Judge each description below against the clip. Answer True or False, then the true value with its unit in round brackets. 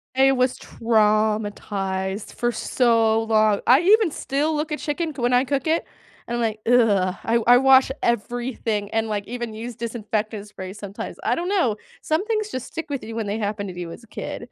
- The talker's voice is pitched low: False (230 Hz)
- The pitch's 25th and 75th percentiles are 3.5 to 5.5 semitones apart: True (4.3 semitones)